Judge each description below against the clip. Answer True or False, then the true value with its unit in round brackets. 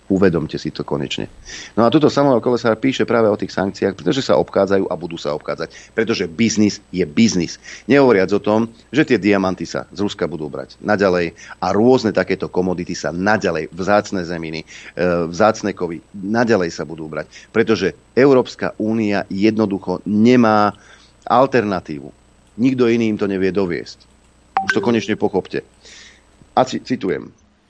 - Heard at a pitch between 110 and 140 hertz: False (100 Hz)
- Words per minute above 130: True (155 wpm)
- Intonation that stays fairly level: False (3.9 semitones)